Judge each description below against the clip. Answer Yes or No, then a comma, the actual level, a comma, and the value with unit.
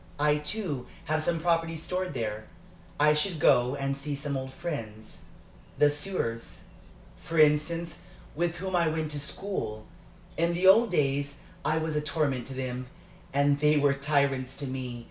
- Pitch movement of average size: Yes, average, 3.5 semitones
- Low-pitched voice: No, medium, 150 Hz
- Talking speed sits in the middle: Yes, average, 165 wpm